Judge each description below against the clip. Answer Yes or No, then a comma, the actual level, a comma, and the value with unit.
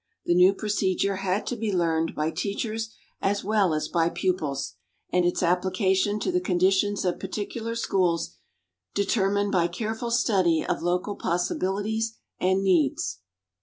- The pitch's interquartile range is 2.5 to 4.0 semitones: Yes, average, 2.9 semitones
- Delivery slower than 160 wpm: Yes, average, 140 wpm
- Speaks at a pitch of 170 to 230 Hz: Yes, high, 190 Hz